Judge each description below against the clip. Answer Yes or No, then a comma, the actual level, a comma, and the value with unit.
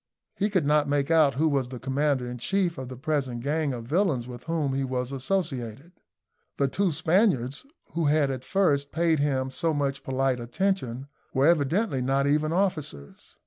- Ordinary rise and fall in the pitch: Yes, average, 3.8 semitones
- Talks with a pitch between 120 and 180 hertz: Yes, medium, 140 Hz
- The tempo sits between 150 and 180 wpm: Yes, average, 175 wpm